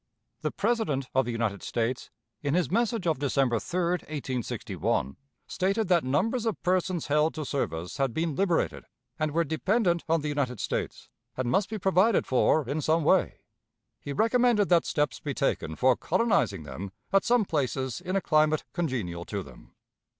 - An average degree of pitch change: No, wide, 6.3 semitones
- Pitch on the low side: No, medium, 155 Hz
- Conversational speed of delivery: Yes, average, 170 wpm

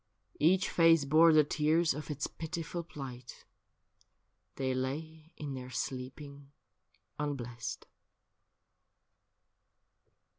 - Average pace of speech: No, slow, 90 wpm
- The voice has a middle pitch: Yes, medium, 150 Hz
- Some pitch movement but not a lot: Yes, average, 3.5 semitones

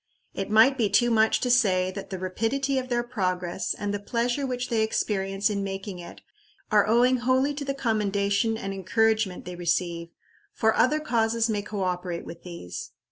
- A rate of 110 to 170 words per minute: No, average, 185 wpm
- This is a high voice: Yes, high, 215 Hz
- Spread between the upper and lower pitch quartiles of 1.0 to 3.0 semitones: No, average, 4.1 semitones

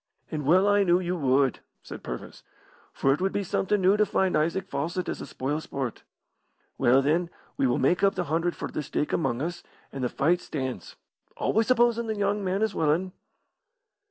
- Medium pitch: Yes, medium, 175 Hz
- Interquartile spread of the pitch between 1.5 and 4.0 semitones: No, wide, 5.6 semitones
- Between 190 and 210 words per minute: Yes, average, 195 wpm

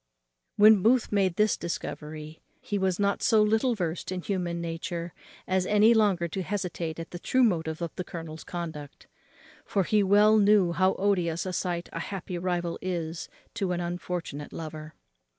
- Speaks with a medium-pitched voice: Yes, medium, 180 Hz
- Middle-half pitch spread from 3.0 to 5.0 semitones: Yes, average, 3.3 semitones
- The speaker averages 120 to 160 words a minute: No, average, 170 wpm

